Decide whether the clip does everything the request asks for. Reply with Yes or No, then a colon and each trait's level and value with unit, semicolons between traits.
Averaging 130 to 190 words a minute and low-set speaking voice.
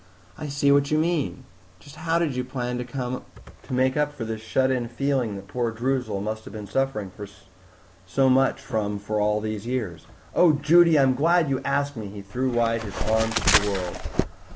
No: average, 200 wpm; low, 125 Hz